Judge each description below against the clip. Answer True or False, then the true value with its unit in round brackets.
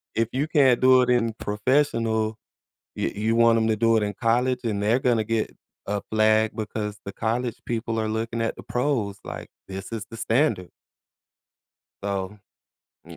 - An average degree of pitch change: False (2.1 semitones)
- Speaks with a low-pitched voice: True (115 Hz)